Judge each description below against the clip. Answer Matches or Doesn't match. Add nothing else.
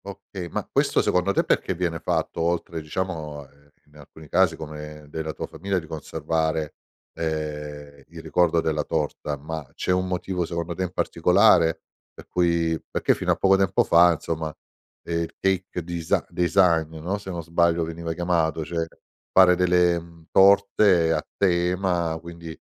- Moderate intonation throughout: Doesn't match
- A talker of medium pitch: Doesn't match